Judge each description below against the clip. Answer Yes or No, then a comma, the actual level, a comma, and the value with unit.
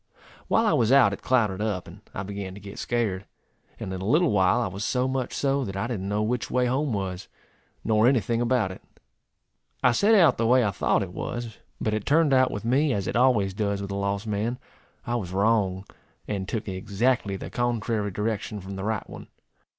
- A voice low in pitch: Yes, low, 110 Hz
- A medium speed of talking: No, fast, 220 wpm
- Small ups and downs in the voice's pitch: No, average, 3.9 semitones